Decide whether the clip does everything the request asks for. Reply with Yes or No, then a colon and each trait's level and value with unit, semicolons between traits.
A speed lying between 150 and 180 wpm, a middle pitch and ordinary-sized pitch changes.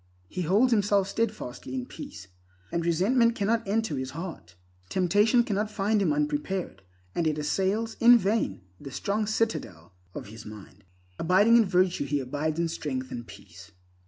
No: average, 160 wpm; medium, 180 Hz; wide, 7.2 semitones